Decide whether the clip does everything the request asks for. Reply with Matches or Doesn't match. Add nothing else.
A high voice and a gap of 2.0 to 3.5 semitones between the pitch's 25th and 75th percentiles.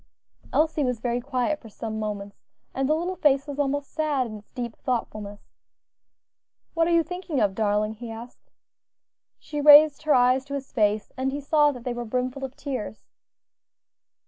Doesn't match